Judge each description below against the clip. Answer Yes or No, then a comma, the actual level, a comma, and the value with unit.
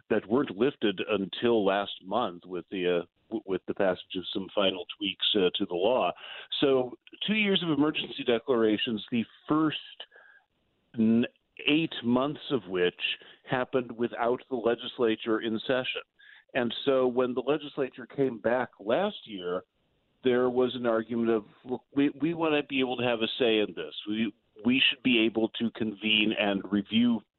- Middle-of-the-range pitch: No, low, 120 Hz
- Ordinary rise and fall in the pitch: Yes, average, 3.9 semitones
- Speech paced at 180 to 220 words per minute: No, average, 165 wpm